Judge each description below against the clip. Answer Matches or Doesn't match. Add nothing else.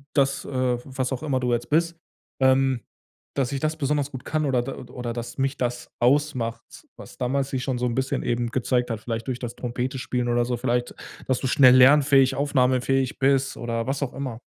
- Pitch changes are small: Matches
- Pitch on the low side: Matches